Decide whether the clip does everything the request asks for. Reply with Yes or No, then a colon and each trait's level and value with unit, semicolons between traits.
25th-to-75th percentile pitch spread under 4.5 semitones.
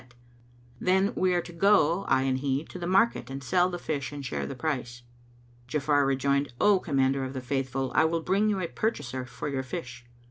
No: average, 5.0 semitones